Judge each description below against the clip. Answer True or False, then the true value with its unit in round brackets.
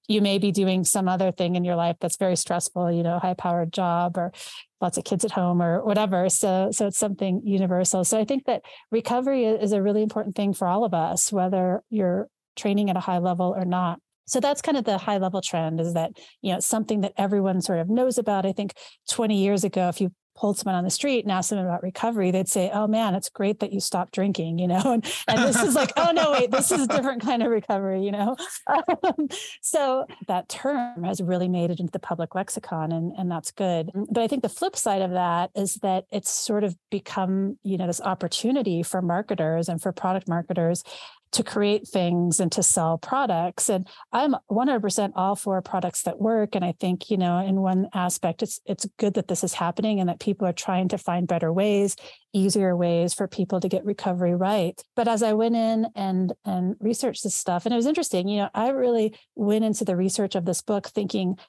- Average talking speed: False (225 wpm)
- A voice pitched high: True (195 Hz)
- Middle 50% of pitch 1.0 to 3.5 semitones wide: True (3.2 semitones)